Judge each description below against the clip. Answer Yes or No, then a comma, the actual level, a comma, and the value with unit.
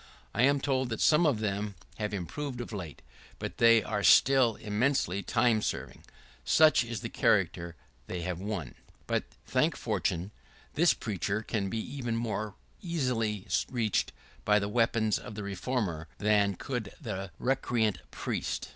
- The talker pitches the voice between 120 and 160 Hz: No, low, 110 Hz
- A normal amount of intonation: Yes, average, 3.6 semitones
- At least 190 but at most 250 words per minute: No, average, 155 wpm